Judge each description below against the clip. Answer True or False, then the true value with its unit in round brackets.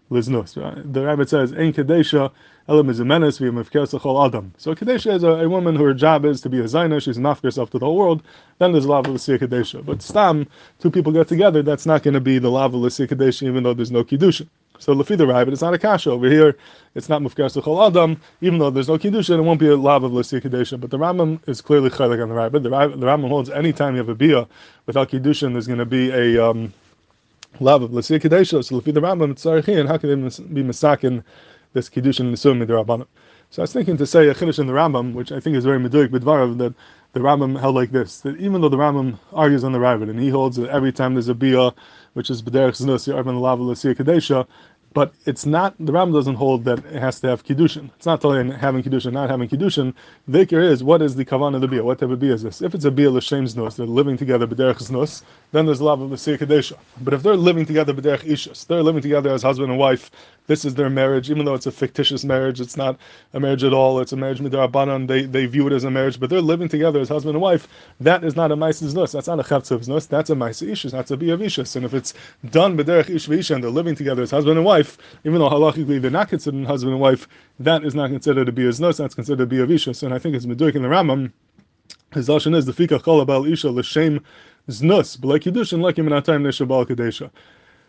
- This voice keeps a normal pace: False (240 wpm)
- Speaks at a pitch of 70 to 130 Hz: False (140 Hz)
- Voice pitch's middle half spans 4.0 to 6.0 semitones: False (3.1 semitones)